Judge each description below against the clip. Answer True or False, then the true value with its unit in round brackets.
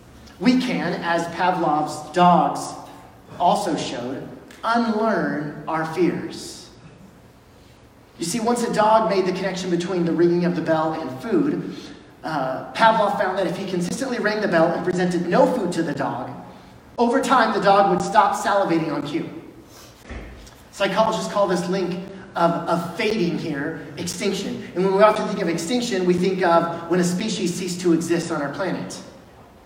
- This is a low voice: False (180 Hz)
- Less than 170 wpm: True (160 wpm)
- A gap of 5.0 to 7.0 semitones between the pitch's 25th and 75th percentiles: False (3.5 semitones)